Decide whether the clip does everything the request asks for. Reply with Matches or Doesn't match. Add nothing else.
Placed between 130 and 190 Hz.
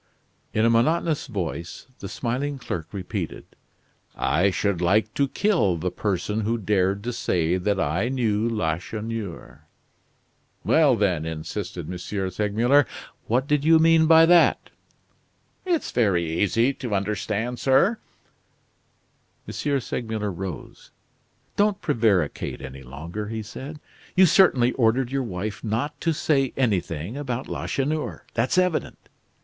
Doesn't match